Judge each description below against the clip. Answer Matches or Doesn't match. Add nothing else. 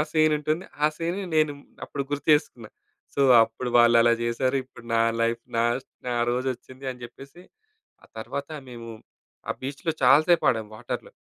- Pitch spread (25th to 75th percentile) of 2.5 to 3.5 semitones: Doesn't match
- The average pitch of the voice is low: Matches